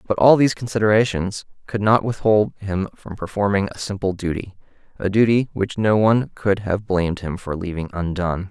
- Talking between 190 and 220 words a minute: No, average, 170 wpm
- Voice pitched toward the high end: No, low, 100 Hz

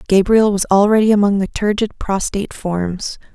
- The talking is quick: No, average, 145 wpm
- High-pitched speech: Yes, high, 200 Hz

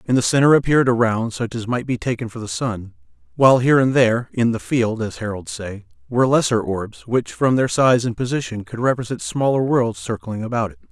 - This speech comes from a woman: No, male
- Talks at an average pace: No, fast, 220 wpm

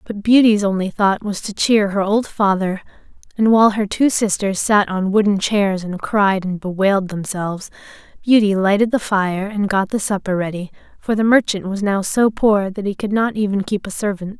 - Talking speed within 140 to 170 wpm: No, average, 200 wpm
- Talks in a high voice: Yes, high, 200 Hz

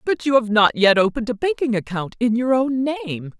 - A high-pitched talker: Yes, high, 235 Hz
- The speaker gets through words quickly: Yes, fast, 230 wpm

